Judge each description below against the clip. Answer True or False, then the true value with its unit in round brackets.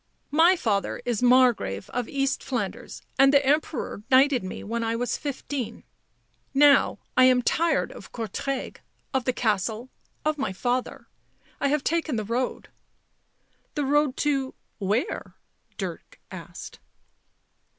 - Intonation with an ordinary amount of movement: True (3.6 semitones)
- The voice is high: True (255 Hz)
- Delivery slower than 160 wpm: True (145 wpm)